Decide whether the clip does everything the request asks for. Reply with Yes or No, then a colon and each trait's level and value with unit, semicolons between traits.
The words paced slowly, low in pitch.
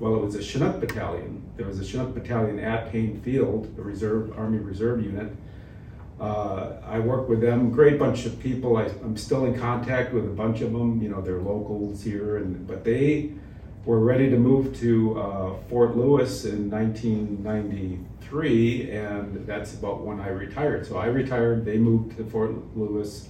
No: average, 185 wpm; low, 110 Hz